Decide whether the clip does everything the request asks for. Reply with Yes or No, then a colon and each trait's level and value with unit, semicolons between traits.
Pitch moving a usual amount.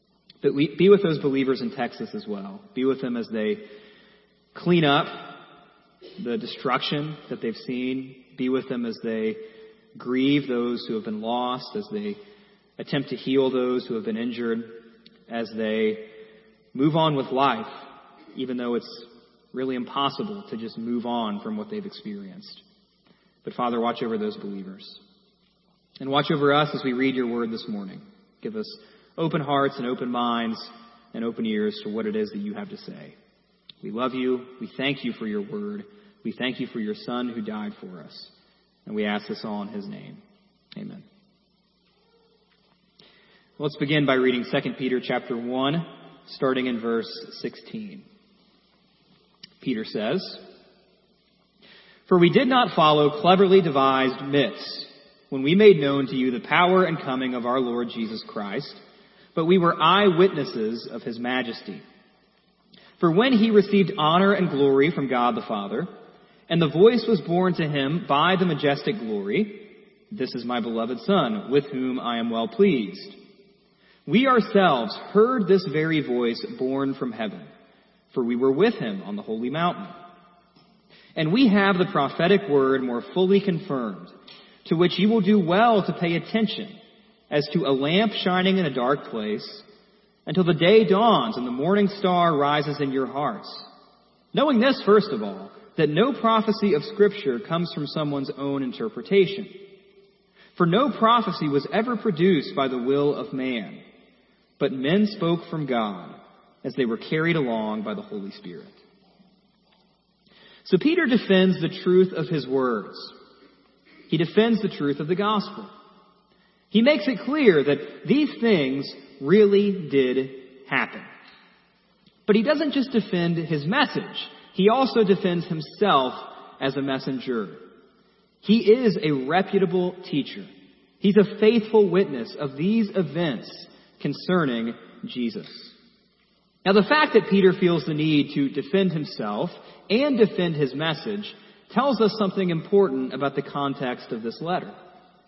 No: wide, 6.9 semitones